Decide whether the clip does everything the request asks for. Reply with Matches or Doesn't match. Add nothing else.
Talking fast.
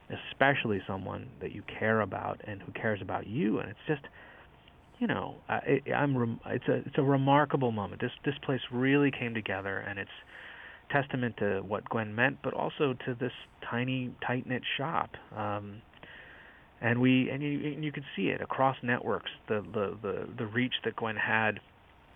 Doesn't match